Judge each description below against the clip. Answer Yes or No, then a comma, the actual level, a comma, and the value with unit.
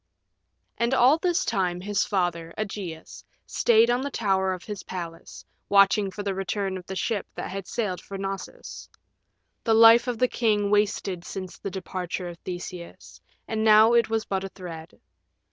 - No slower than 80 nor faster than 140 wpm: No, average, 170 wpm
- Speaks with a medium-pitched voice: No, high, 195 Hz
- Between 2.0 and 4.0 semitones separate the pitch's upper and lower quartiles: Yes, average, 3.2 semitones